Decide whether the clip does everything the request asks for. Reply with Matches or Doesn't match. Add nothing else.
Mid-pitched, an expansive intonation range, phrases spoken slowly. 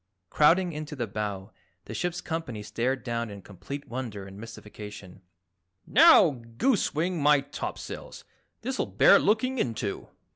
Doesn't match